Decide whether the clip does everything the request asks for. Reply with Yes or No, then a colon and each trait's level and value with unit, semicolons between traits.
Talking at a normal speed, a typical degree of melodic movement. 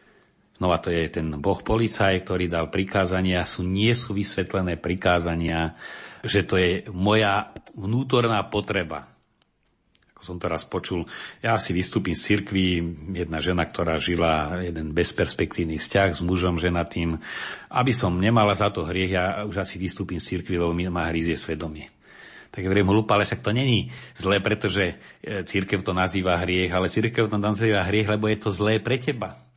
No: fast, 170 wpm; average, 3.1 semitones